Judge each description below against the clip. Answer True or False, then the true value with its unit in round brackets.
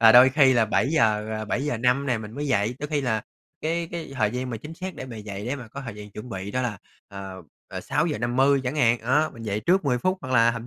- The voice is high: False (125 Hz)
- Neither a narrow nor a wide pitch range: True (4.3 semitones)